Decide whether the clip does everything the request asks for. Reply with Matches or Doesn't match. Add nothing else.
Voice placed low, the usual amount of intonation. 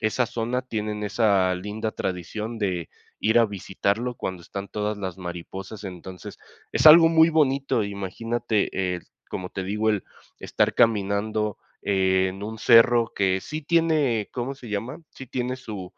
Matches